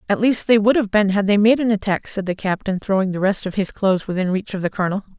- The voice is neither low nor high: No, high, 200 Hz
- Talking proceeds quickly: Yes, fast, 290 wpm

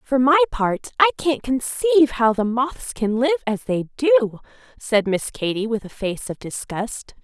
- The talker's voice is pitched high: Yes, very high, 250 Hz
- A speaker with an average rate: Yes, average, 180 wpm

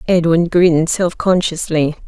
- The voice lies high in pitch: No, medium, 170 Hz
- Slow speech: Yes, slow, 115 wpm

